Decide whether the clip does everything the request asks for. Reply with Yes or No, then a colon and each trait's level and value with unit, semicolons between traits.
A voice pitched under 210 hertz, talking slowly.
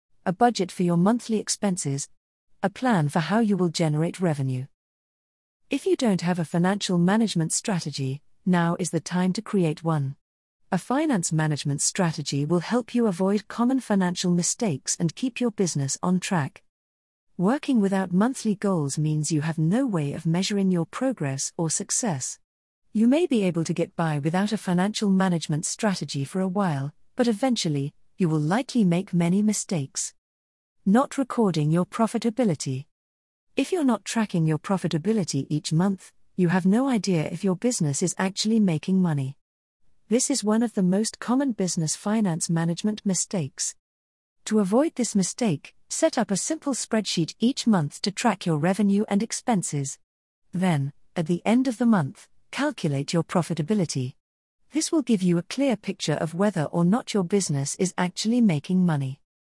No: medium, 185 Hz; average, 165 wpm